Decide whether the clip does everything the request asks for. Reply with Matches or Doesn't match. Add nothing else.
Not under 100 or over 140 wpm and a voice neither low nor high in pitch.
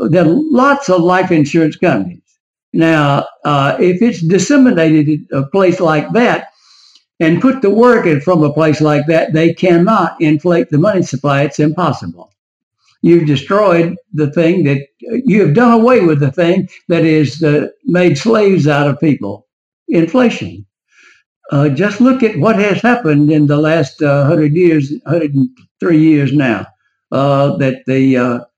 Doesn't match